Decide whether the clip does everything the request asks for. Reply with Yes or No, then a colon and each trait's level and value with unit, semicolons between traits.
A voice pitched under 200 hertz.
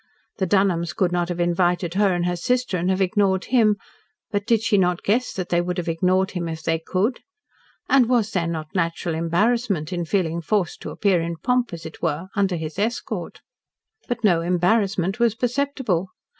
Yes: medium, 185 Hz